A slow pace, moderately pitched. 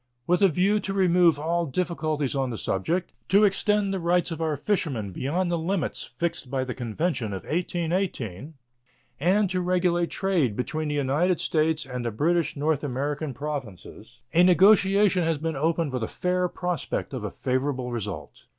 No: average, 170 wpm; medium, 160 Hz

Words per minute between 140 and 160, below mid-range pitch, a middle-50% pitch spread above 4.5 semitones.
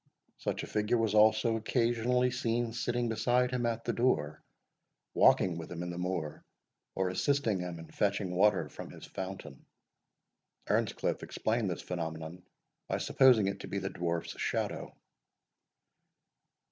Yes: average, 145 wpm; low, 105 Hz; average, 4.9 semitones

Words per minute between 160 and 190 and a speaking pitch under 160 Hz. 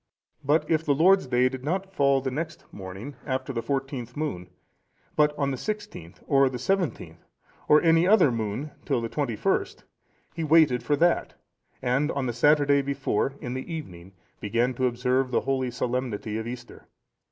Yes: average, 175 wpm; low, 135 Hz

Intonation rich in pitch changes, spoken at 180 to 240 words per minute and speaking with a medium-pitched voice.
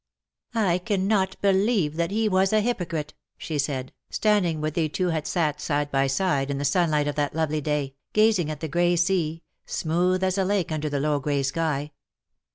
No: average, 4.2 semitones; average, 195 wpm; medium, 165 Hz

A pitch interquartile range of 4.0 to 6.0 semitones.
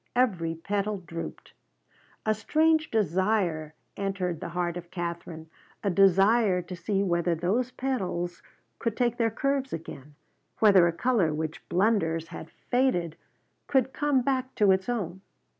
Yes: wide, 5.4 semitones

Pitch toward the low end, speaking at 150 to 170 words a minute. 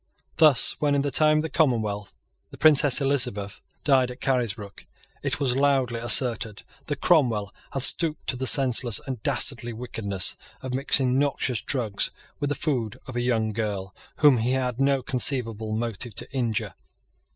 Yes: low, 125 Hz; average, 165 wpm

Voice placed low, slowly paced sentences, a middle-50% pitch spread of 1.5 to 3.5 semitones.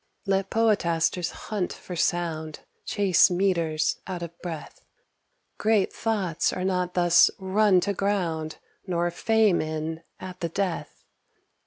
No: medium, 180 Hz; slow, 125 wpm; average, 2.8 semitones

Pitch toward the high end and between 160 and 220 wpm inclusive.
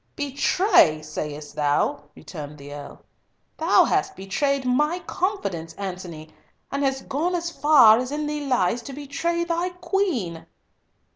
No: very high, 265 Hz; slow, 135 wpm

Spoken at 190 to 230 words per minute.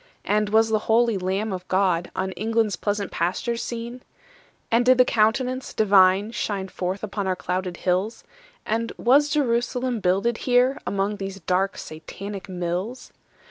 No: average, 145 wpm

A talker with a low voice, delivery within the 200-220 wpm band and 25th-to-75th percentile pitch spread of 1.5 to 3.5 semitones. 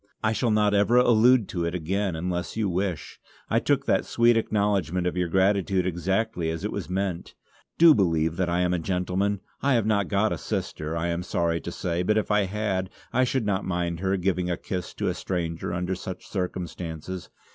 Yes: very low, 95 Hz; fast, 205 wpm; average, 3.0 semitones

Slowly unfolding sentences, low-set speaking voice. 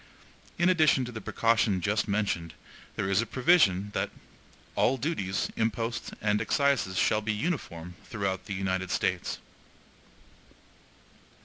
Yes: slow, 125 wpm; low, 105 Hz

